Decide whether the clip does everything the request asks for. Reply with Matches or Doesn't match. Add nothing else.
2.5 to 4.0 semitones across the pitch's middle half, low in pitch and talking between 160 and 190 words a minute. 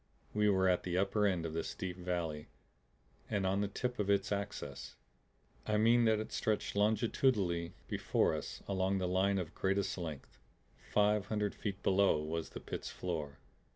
Matches